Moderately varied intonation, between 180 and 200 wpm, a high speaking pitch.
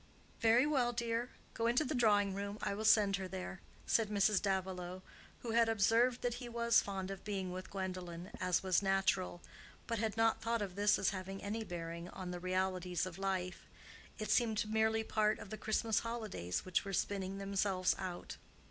Yes: average, 3.2 semitones; average, 185 wpm; high, 200 Hz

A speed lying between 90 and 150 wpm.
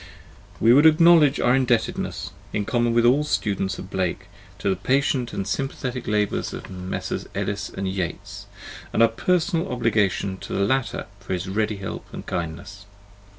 No: average, 160 wpm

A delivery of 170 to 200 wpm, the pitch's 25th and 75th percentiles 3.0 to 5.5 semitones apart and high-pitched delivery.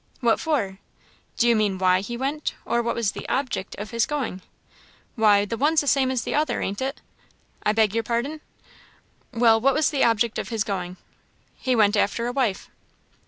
Yes: average, 195 wpm; average, 4.3 semitones; high, 235 Hz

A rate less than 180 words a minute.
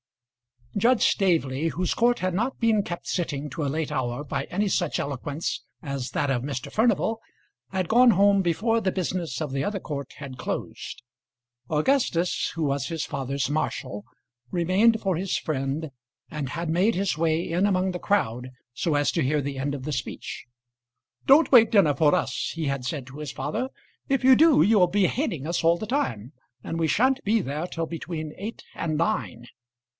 No: average, 190 wpm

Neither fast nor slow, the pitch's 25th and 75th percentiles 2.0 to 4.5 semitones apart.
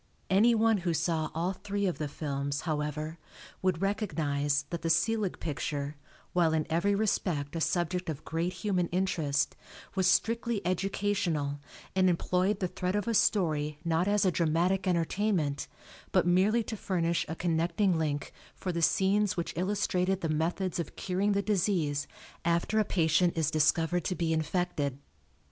Yes: average, 155 wpm; average, 3.4 semitones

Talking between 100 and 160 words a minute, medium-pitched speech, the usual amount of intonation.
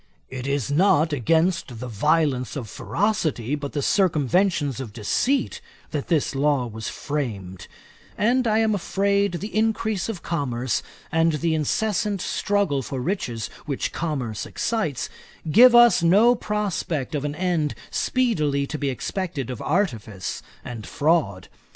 No: average, 140 wpm; medium, 155 Hz; wide, 7.1 semitones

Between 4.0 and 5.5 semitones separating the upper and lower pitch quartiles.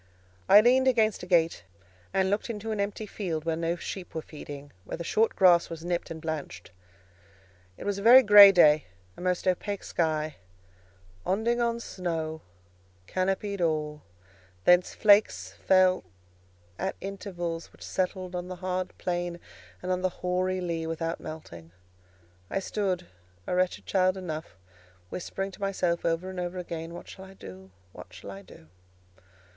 No: average, 3.0 semitones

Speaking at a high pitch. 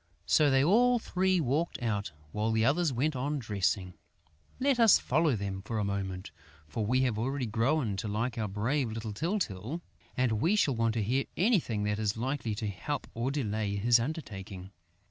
No: low, 115 Hz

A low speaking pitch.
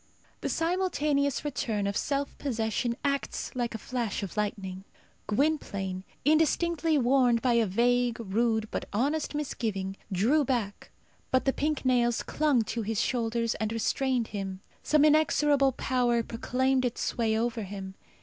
No: high, 240 Hz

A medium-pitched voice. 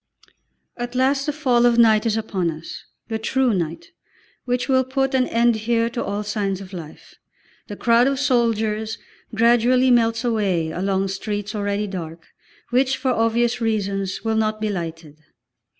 No: high, 220 Hz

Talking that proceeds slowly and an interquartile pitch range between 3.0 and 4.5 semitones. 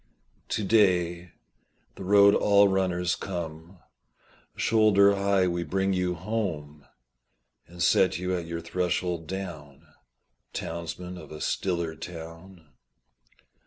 No: slow, 110 wpm; narrow, 2.5 semitones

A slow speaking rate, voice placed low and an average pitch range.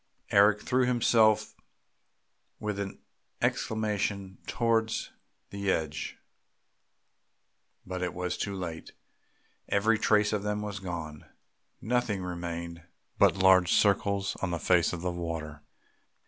Yes: slow, 115 wpm; very low, 95 Hz; average, 3.3 semitones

